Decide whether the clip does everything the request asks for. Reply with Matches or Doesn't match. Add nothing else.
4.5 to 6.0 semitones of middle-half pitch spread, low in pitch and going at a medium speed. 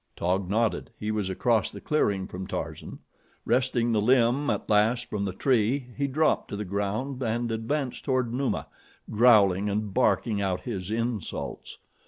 Doesn't match